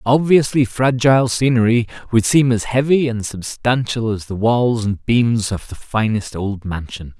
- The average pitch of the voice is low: Yes, low, 115 Hz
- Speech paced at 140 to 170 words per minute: Yes, average, 160 wpm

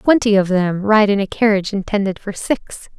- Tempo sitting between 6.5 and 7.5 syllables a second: No, 5.2 syllables/s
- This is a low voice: No, high, 205 Hz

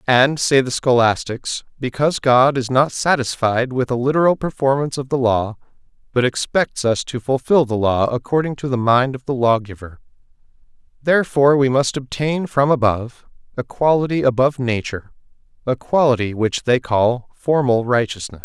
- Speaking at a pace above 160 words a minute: No, average, 155 wpm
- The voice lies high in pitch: No, low, 130 Hz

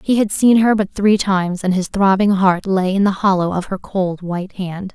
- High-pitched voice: Yes, high, 195 Hz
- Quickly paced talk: Yes, fast, 230 wpm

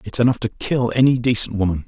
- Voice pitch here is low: Yes, low, 115 Hz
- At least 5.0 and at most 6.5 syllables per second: Yes, 6.4 syllables/s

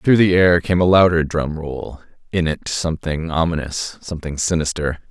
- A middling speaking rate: Yes, average, 155 wpm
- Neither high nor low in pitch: No, very low, 80 Hz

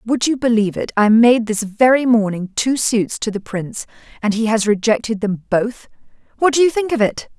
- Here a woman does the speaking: Yes, female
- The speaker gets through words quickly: Yes, fast, 210 wpm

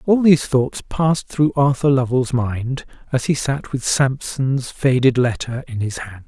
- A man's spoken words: Yes, male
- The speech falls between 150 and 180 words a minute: Yes, average, 170 wpm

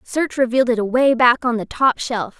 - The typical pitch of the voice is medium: No, high, 245 Hz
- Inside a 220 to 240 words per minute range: Yes, fast, 225 wpm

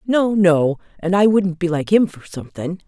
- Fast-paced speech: Yes, fast, 210 wpm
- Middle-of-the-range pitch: Yes, medium, 180 Hz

